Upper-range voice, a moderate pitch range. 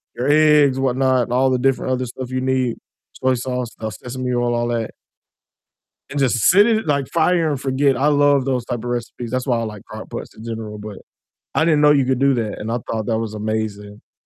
No: low, 130 Hz; average, 3.0 semitones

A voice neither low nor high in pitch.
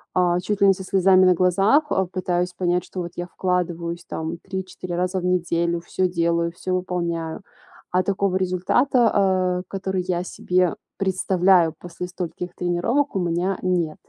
Yes: medium, 180 Hz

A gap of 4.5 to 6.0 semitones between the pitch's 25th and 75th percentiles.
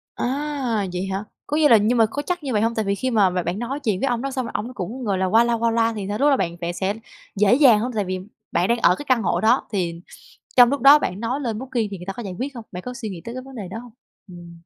Yes: average, 4.8 semitones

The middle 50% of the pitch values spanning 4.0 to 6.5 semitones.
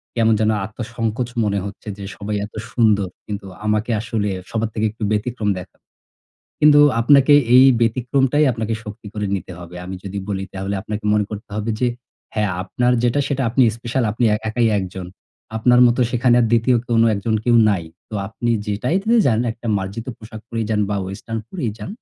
No: average, 2.7 semitones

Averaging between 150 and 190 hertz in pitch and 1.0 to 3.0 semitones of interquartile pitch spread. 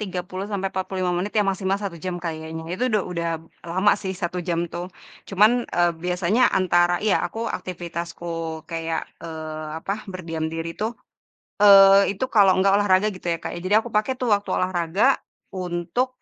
Yes: medium, 185 Hz; average, 2.7 semitones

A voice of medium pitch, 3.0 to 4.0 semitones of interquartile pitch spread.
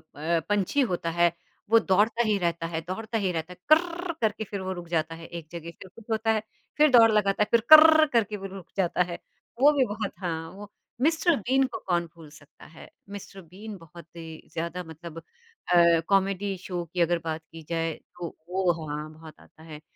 No: medium, 180 Hz; average, 4.7 semitones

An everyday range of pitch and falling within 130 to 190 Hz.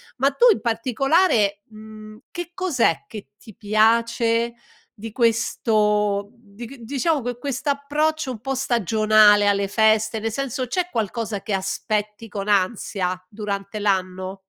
No: average, 3.3 semitones; high, 220 Hz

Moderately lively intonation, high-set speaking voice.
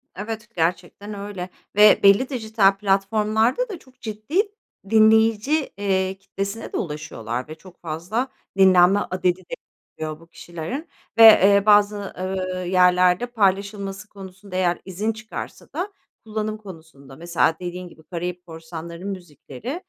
Yes: average, 3.5 semitones; high, 195 Hz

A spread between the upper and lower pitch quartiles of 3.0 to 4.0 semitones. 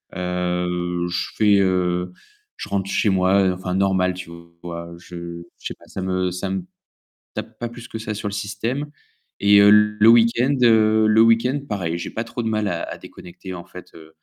Yes: average, 3.3 semitones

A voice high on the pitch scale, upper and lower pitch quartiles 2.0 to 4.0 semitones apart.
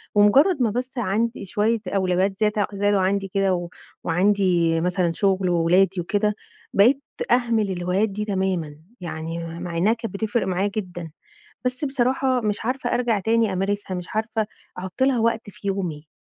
Yes: high, 200 Hz; average, 3.7 semitones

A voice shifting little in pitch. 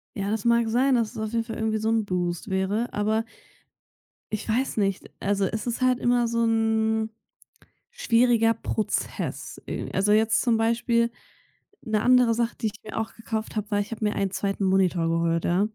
Yes: narrow, 2.3 semitones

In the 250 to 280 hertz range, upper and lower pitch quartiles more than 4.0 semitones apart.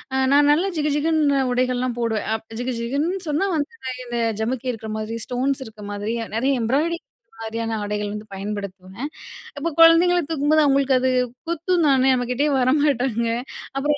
Yes: very high, 260 Hz; average, 4.6 semitones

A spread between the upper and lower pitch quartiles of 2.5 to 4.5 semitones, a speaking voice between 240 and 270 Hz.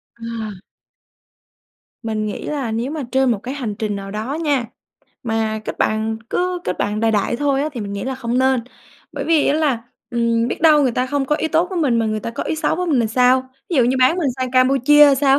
Yes: average, 4.2 semitones; very high, 255 Hz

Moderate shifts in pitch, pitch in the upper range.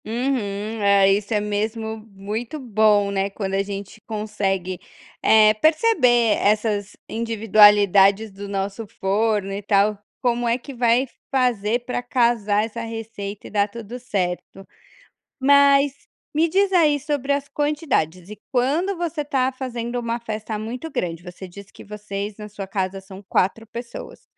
Yes: average, 3.6 semitones; high, 215 Hz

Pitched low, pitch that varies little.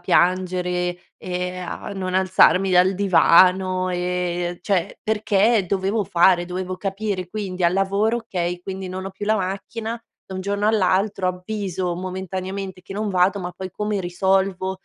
No: medium, 185 Hz; narrow, 1.5 semitones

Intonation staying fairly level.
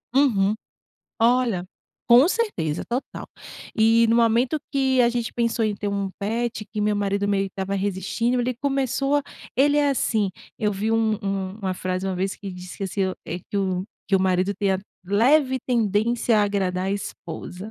No: average, 3.8 semitones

